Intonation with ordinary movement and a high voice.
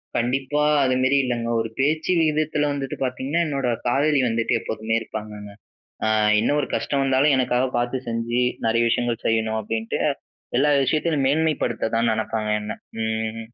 No: average, 3.8 semitones; low, 125 Hz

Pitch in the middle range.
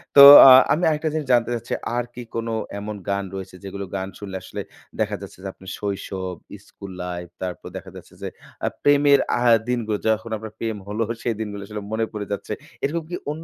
No: low, 105 Hz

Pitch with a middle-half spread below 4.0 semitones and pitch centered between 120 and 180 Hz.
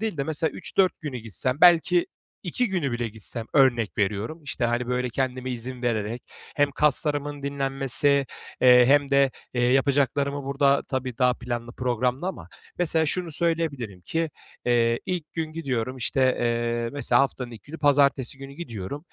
Yes: average, 3.3 semitones; low, 135 Hz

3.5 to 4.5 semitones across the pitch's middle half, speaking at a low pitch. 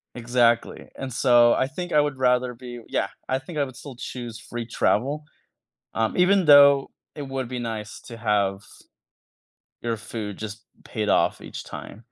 No: average, 3.0 semitones; low, 125 Hz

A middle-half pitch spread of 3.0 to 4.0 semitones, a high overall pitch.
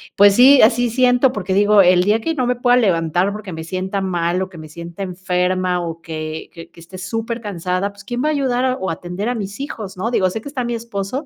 No: average, 5.0 semitones; high, 200 Hz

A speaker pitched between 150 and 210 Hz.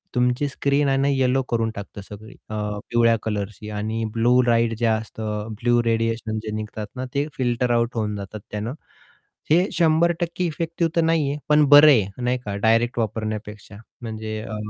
No: low, 115 Hz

